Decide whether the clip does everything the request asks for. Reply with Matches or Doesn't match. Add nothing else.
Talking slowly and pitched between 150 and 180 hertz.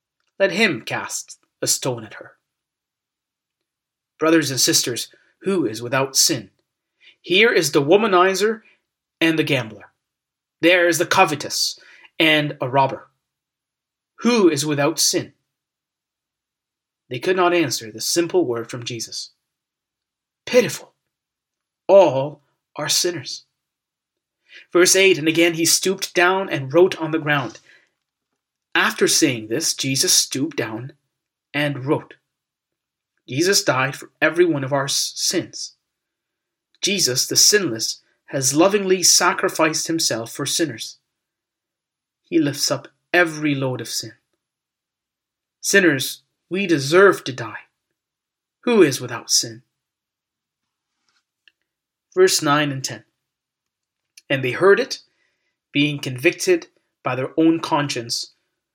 Matches